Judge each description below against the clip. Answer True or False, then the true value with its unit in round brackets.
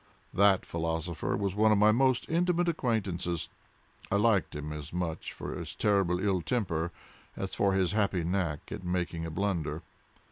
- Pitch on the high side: False (95 Hz)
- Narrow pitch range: False (3.8 semitones)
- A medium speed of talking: True (165 wpm)